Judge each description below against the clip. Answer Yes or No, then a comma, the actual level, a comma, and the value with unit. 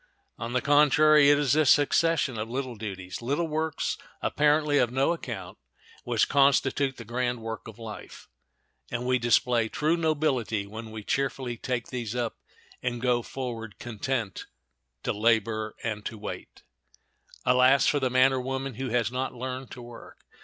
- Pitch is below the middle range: Yes, low, 125 Hz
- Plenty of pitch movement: No, average, 3.3 semitones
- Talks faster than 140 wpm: Yes, average, 155 wpm